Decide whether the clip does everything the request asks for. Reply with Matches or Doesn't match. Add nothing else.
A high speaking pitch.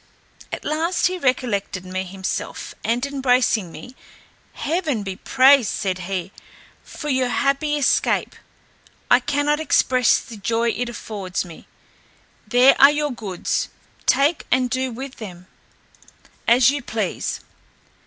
Matches